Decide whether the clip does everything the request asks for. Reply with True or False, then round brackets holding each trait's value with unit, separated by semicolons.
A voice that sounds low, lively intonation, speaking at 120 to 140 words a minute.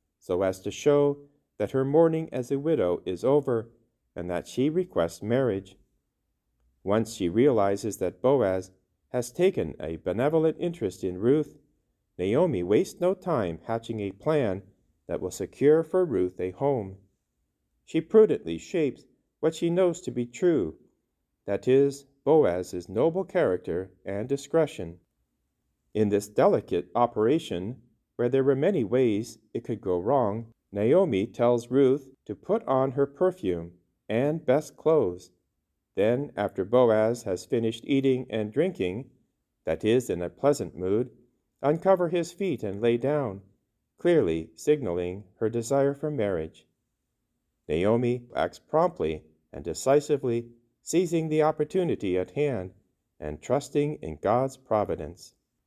True (115 Hz; 7.7 semitones; 135 wpm)